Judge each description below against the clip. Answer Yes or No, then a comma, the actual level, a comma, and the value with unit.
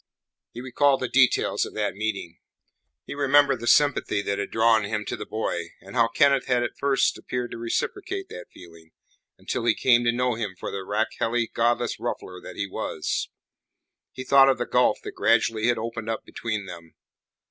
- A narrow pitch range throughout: No, average, 3.5 semitones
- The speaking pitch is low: Yes, low, 115 Hz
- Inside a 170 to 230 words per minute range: Yes, average, 190 wpm